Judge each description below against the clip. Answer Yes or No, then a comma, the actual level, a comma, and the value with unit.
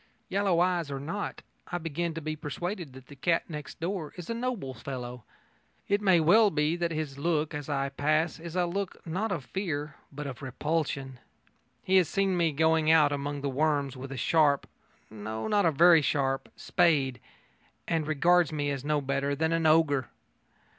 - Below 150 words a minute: No, average, 185 wpm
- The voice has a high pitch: No, medium, 155 Hz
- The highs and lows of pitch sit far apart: No, average, 3.6 semitones